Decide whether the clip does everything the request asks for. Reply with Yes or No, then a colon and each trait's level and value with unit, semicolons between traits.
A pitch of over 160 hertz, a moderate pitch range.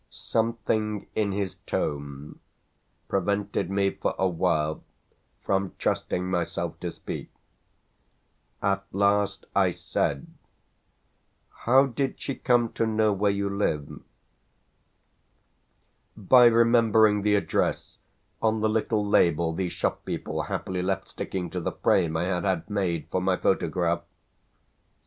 No: low, 100 Hz; average, 3.4 semitones